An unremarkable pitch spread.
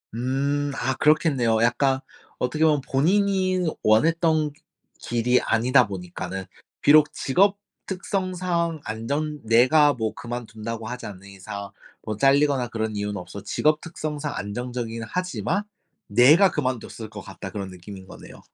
No: wide, 5.8 semitones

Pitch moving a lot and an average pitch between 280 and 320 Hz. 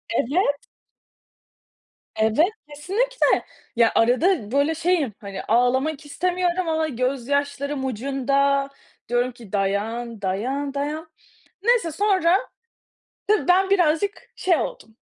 Yes: wide, 6.0 semitones; very high, 285 Hz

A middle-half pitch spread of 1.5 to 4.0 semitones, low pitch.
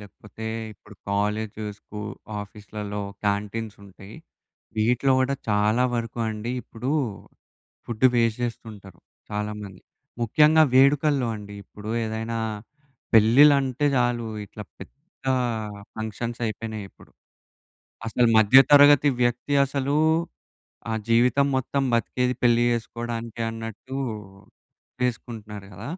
Yes: average, 3.0 semitones; low, 115 Hz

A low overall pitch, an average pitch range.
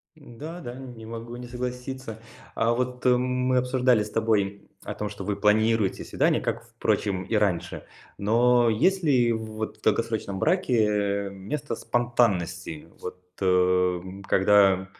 Yes: low, 110 Hz; average, 3.9 semitones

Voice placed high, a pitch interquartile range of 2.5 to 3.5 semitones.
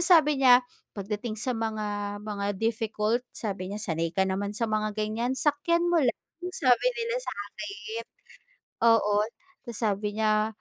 Yes: high, 215 Hz; average, 2.9 semitones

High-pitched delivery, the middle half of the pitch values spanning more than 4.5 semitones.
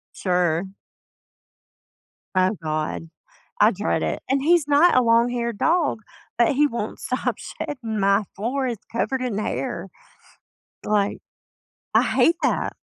Yes: high, 235 Hz; average, 5.3 semitones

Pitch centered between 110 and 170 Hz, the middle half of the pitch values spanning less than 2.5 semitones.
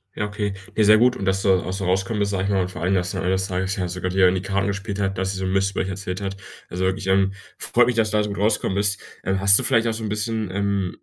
No: very low, 95 Hz; narrow, 1.7 semitones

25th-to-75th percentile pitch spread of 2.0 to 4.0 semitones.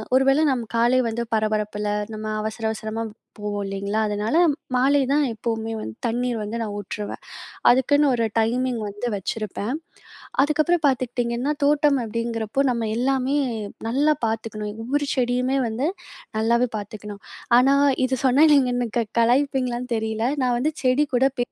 Yes: average, 3.3 semitones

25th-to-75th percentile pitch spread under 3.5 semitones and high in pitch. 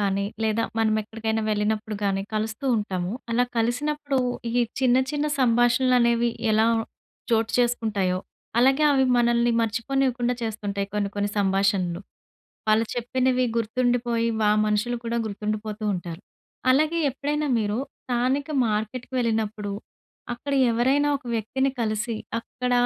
Yes: average, 2.9 semitones; high, 230 Hz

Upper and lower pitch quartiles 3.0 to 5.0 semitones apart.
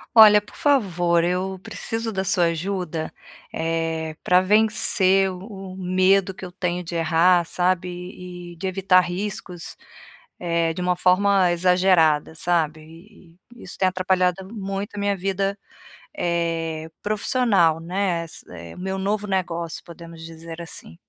No: narrow, 2.5 semitones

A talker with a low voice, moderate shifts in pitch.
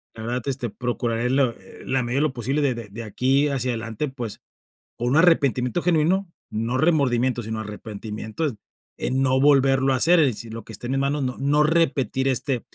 Yes: low, 130 Hz; average, 3.2 semitones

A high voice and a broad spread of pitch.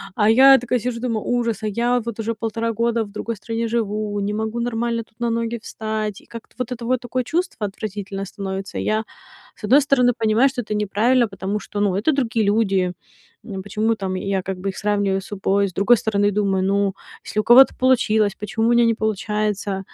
No: high, 220 Hz; narrow, 2.6 semitones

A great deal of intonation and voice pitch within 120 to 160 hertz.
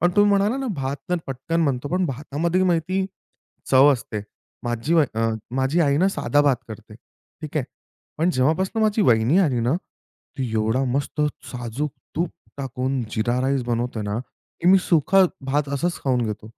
Yes: wide, 5.8 semitones; medium, 140 Hz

